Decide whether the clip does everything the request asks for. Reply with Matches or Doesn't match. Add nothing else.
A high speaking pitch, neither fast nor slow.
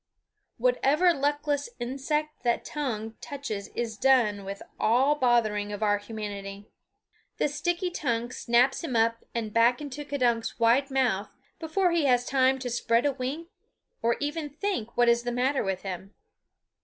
Matches